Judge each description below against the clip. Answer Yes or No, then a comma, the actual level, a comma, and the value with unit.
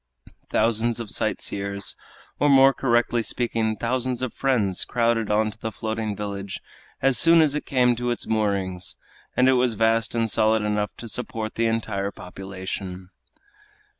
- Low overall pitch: Yes, low, 110 Hz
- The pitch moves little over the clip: No, average, 3.0 semitones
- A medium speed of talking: Yes, average, 160 wpm